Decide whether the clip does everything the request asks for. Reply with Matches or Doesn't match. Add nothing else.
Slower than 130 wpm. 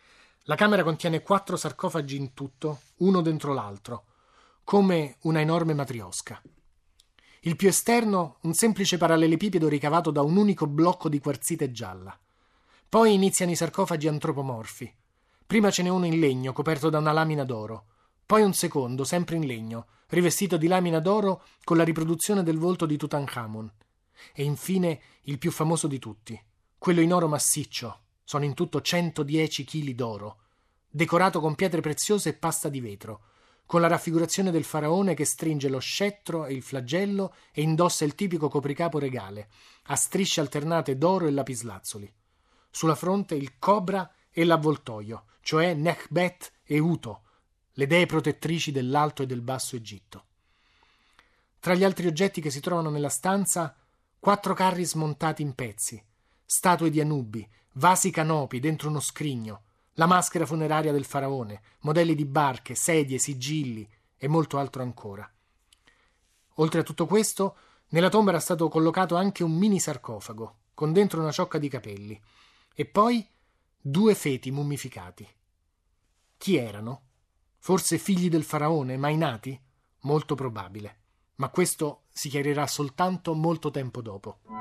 Doesn't match